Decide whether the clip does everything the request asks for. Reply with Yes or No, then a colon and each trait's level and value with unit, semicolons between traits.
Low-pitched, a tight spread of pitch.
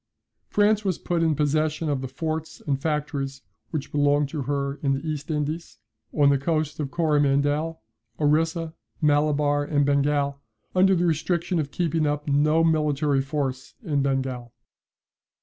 No: medium, 150 Hz; narrow, 2.2 semitones